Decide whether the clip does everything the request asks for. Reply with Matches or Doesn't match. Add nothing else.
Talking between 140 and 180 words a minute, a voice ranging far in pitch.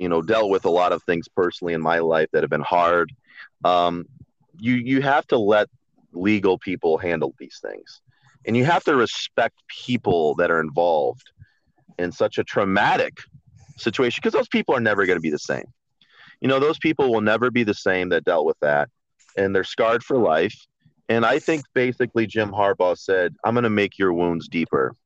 Doesn't match